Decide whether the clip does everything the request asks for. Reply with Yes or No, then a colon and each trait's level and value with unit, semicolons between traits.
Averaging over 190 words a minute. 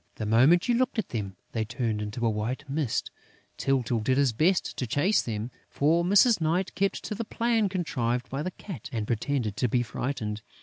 Yes: average, 200 wpm